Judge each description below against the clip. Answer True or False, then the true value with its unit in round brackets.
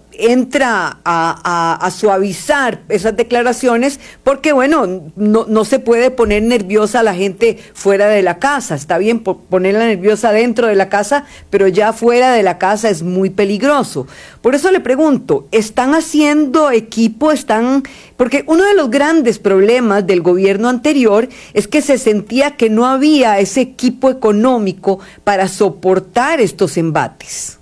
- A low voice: False (225 Hz)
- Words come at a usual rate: True (150 wpm)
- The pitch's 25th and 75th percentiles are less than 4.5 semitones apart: False (4.8 semitones)